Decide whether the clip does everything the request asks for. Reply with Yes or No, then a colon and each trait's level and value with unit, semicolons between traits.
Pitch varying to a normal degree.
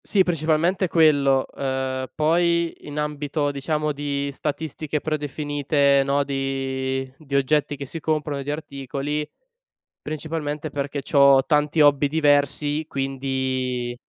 No: narrow, 2.0 semitones